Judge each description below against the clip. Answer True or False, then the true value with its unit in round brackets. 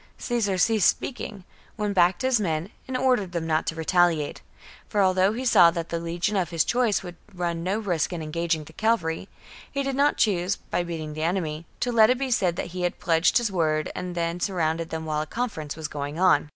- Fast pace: True (220 wpm)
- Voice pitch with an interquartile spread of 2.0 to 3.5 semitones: False (4.3 semitones)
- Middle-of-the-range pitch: True (175 Hz)